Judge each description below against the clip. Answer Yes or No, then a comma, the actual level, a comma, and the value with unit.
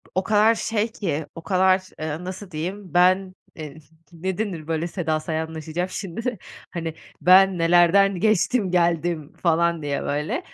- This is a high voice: No, medium, 175 Hz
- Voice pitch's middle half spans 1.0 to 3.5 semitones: Yes, average, 3.1 semitones